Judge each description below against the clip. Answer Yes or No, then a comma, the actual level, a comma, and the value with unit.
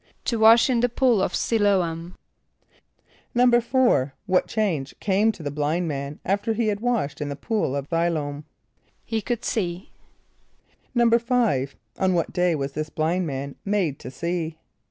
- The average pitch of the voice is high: No, medium, 180 Hz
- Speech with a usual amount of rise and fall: No, wide, 7.0 semitones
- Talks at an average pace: Yes, average, 160 wpm